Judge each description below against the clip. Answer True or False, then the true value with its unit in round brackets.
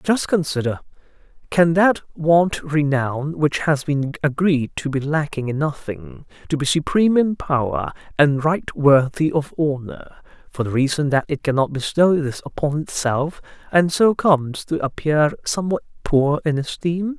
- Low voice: False (150 Hz)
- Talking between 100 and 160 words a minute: True (155 wpm)